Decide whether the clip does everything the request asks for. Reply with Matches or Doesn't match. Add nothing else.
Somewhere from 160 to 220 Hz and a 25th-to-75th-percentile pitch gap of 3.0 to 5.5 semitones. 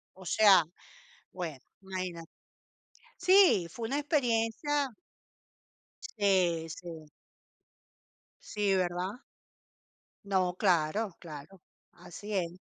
Matches